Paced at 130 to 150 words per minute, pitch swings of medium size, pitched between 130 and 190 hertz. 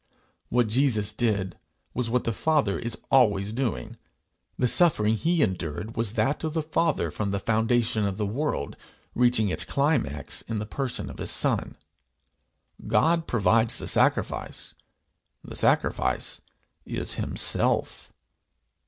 No: slow, 135 wpm; average, 4.6 semitones; low, 115 Hz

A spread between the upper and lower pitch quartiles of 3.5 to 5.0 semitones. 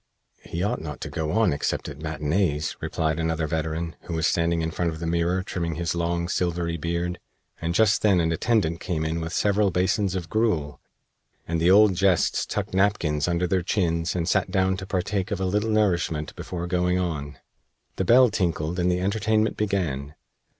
No: average, 2.7 semitones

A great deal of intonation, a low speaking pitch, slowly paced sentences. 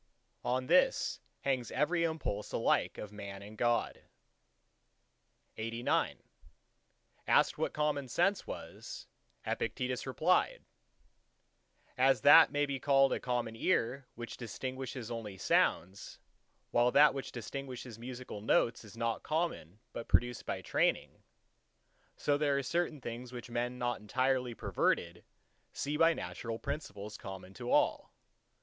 No: average, 3.3 semitones; low, 125 Hz; slow, 130 wpm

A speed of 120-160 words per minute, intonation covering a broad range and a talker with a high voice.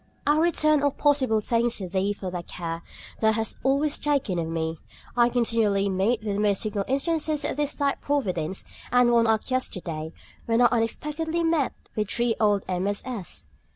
No: average, 170 wpm; wide, 6.0 semitones; high, 225 Hz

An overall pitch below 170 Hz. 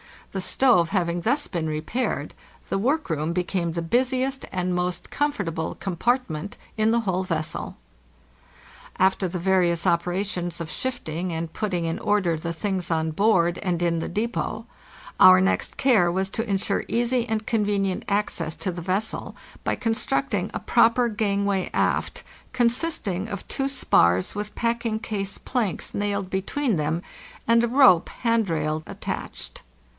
No: high, 195 Hz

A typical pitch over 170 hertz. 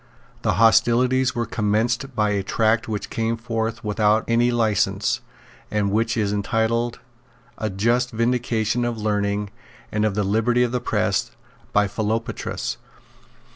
No: low, 110 Hz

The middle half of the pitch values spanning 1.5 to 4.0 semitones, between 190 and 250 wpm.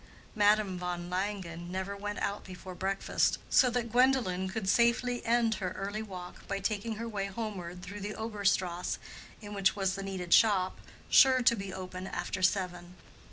No: average, 2.7 semitones; average, 170 wpm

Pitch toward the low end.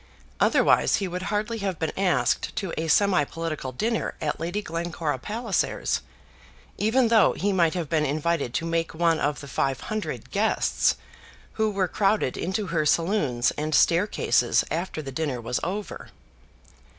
No: medium, 170 Hz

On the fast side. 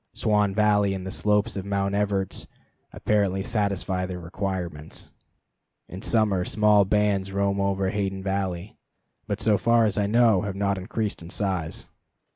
No: average, 150 wpm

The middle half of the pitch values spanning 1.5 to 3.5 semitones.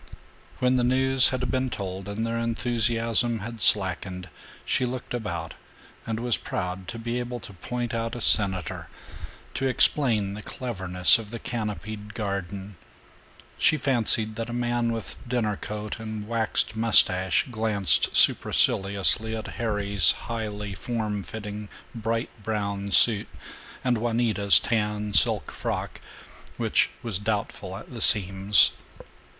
Yes: average, 2.7 semitones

